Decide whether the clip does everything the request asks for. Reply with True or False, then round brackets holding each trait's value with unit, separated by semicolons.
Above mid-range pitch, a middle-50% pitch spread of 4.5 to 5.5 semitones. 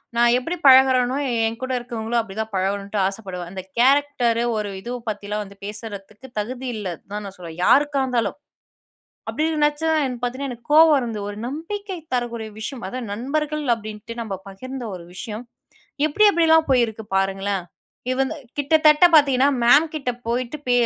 True (240 Hz; 4.9 semitones)